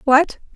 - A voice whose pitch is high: Yes, very high, 290 Hz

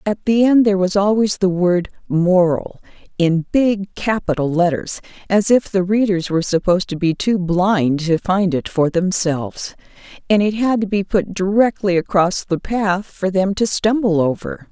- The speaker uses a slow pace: No, average, 175 wpm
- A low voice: No, high, 190 Hz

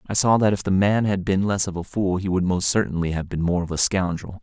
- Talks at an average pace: No, fast, 300 wpm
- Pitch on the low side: Yes, very low, 95 Hz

